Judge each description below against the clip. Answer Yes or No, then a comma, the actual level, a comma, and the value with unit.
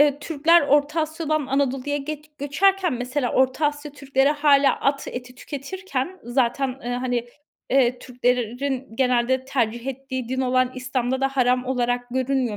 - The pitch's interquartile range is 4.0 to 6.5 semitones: No, narrow, 2.5 semitones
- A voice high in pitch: Yes, very high, 265 Hz